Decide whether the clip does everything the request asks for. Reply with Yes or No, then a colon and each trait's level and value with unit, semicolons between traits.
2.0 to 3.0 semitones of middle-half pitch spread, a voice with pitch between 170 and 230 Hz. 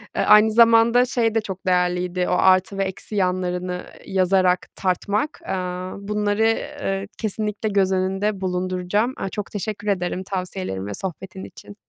Yes: narrow, 2.5 semitones; high, 190 Hz